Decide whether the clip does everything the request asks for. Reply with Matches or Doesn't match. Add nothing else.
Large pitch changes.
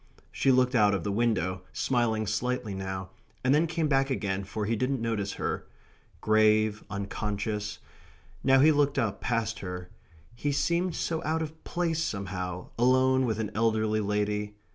Doesn't match